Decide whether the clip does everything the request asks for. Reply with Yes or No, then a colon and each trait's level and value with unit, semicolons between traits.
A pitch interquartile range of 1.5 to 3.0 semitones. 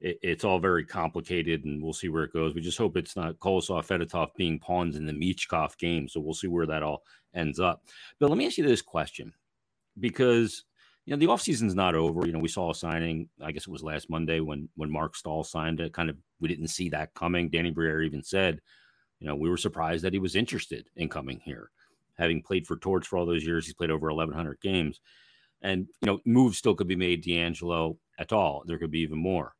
Yes: narrow, 2.4 semitones